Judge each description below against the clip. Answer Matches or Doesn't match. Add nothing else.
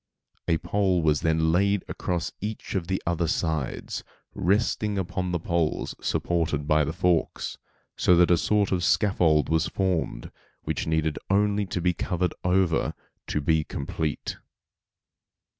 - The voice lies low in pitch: Matches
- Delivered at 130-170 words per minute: Matches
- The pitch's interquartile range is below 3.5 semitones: Matches